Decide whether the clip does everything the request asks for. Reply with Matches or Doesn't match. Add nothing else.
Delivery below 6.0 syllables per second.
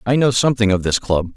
Doesn't match